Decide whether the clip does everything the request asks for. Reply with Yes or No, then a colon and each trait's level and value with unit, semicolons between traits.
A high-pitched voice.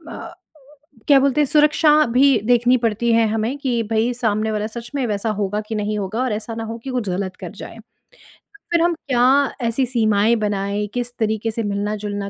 Yes: high, 225 Hz